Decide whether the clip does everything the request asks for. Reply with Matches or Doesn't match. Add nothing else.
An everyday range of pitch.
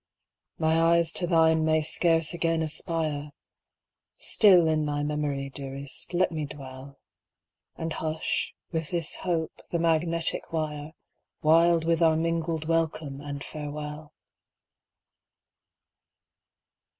Doesn't match